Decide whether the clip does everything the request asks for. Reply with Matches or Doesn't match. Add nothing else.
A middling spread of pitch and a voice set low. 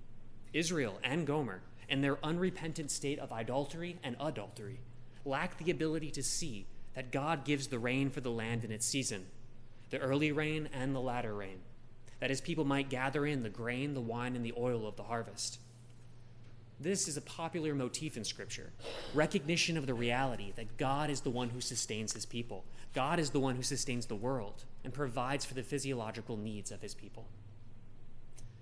Matches